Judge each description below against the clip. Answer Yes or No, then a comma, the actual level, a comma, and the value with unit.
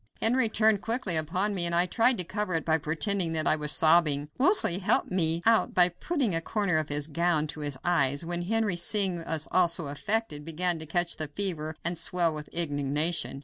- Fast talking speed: Yes, fast, 210 wpm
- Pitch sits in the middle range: Yes, medium, 170 Hz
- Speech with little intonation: No, average, 3.7 semitones